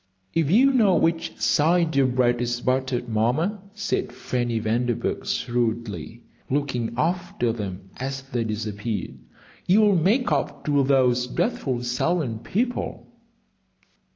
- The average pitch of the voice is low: Yes, low, 130 Hz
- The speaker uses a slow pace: Yes, slow, 120 wpm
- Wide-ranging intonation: Yes, wide, 5.8 semitones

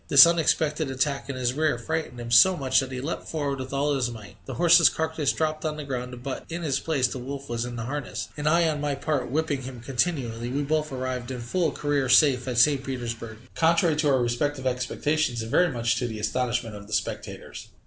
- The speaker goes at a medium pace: No, fast, 225 wpm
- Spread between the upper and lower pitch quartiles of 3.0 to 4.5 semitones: Yes, average, 3.8 semitones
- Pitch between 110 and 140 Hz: Yes, low, 135 Hz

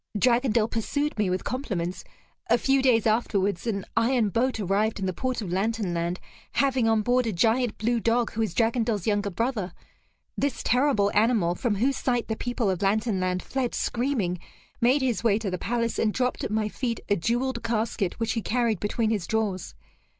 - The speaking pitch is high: Yes, high, 225 Hz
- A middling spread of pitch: Yes, average, 3.2 semitones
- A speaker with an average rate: Yes, average, 190 wpm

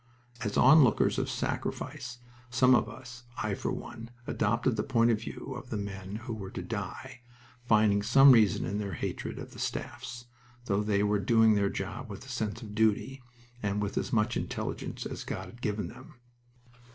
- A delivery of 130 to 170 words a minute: No, average, 185 wpm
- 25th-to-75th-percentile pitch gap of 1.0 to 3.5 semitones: Yes, average, 2.8 semitones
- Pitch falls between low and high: No, low, 110 Hz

